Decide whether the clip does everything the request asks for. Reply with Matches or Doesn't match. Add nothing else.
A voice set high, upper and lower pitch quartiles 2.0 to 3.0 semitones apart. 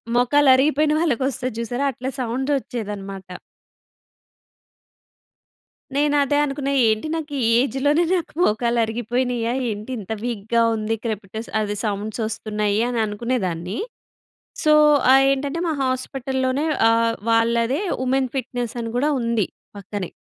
Doesn't match